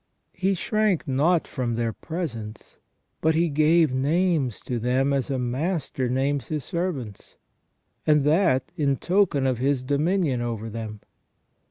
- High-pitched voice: No, medium, 140 Hz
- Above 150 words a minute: No, average, 140 wpm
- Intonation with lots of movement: No, average, 5.0 semitones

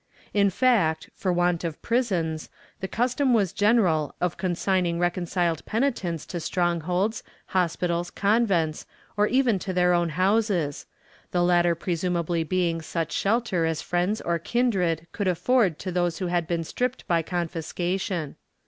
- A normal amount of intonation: Yes, average, 3.0 semitones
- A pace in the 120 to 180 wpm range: Yes, average, 150 wpm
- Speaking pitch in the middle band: Yes, medium, 180 Hz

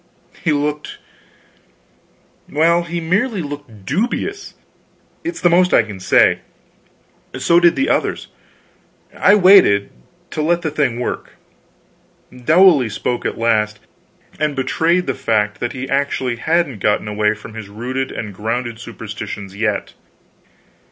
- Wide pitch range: Yes, wide, 7.7 semitones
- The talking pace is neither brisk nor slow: No, slow, 130 wpm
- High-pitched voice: No, low, 135 Hz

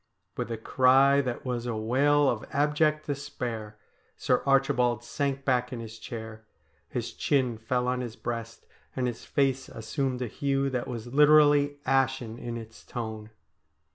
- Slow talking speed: No, average, 160 wpm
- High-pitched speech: No, low, 125 Hz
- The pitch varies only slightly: No, average, 3.0 semitones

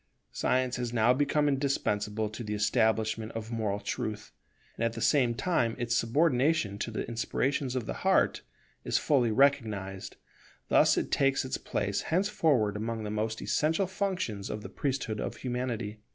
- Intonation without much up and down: No, average, 4.1 semitones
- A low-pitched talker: Yes, low, 115 Hz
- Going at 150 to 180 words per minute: Yes, average, 160 wpm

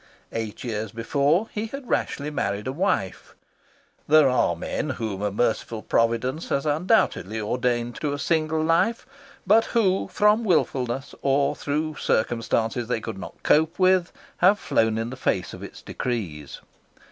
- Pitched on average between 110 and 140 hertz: Yes, low, 135 Hz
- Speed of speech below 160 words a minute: Yes, average, 150 wpm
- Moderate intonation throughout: No, wide, 6.5 semitones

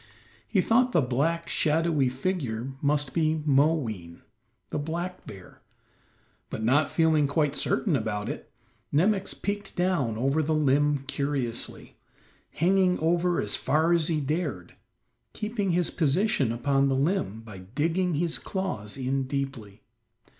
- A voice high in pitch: No, medium, 150 Hz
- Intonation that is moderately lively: Yes, average, 4.6 semitones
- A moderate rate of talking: No, slow, 130 wpm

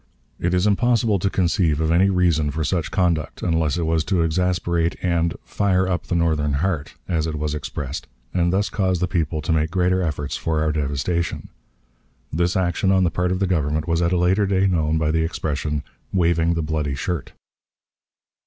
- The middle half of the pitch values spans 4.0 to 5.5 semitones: No, average, 2.8 semitones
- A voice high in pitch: No, very low, 85 Hz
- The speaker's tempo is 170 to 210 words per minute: Yes, average, 190 wpm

